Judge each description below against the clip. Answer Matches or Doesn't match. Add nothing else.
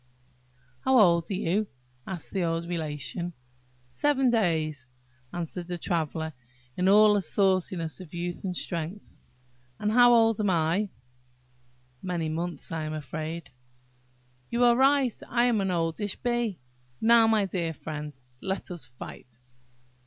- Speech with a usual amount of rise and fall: Matches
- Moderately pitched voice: Matches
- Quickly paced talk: Doesn't match